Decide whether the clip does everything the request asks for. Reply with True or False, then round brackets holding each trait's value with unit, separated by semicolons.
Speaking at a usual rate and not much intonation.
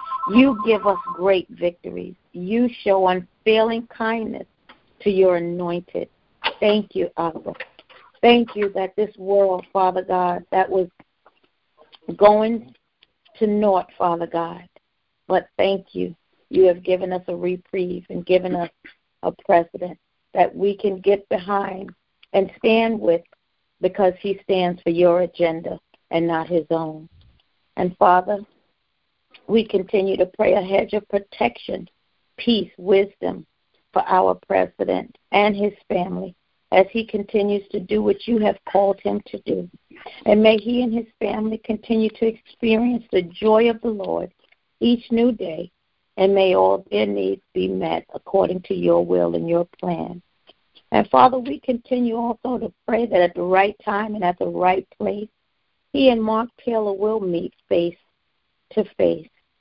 False (150 wpm; 3.5 semitones)